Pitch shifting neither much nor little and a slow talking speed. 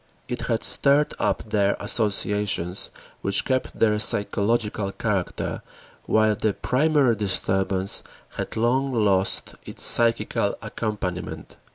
Yes: average, 3.0 semitones; slow, 105 wpm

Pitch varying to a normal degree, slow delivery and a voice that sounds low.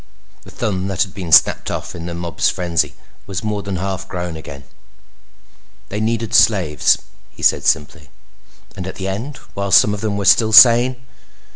No: average, 3.4 semitones; average, 175 wpm; very low, 95 Hz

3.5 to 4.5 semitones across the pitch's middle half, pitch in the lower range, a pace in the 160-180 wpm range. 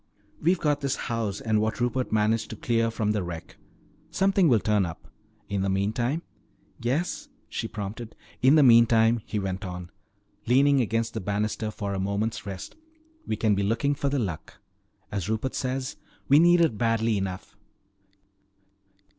Yes: average, 4.1 semitones; low, 115 Hz; average, 165 wpm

